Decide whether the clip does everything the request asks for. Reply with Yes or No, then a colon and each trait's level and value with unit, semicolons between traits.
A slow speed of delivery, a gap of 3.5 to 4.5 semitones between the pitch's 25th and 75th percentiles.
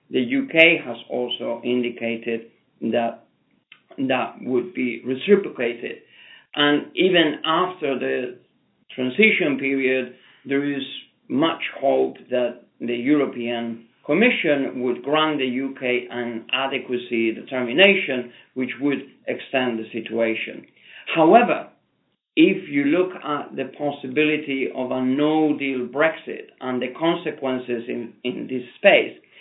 Yes: slow, 110 wpm; average, 3.9 semitones